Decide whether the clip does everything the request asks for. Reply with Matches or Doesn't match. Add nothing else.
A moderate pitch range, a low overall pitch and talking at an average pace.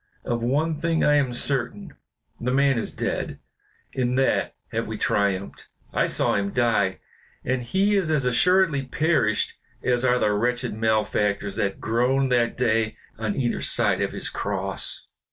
Matches